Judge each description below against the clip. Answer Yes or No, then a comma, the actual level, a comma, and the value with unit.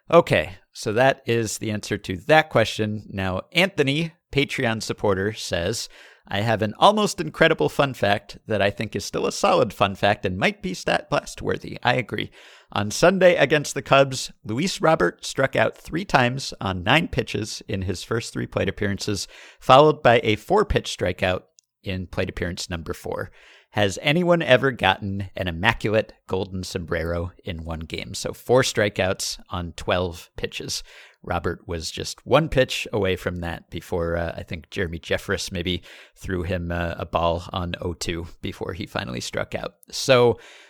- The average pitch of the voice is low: Yes, low, 105 Hz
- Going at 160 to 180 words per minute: Yes, average, 170 wpm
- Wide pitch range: Yes, wide, 6.7 semitones